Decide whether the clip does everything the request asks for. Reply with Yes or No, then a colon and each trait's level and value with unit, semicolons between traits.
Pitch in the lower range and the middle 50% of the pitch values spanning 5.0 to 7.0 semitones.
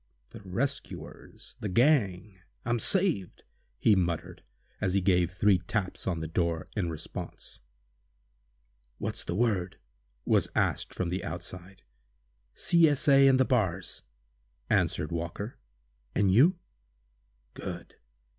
Yes: very low, 95 Hz; average, 5.3 semitones